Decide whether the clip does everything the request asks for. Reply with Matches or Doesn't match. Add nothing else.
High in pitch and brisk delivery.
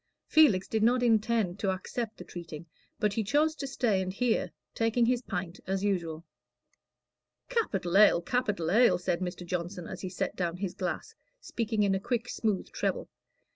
Doesn't match